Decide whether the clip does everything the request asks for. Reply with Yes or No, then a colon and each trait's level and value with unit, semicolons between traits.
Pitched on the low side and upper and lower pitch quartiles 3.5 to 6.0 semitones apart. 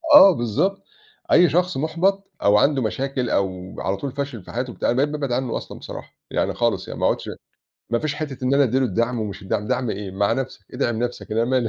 Yes: low, 125 Hz; average, 4.6 semitones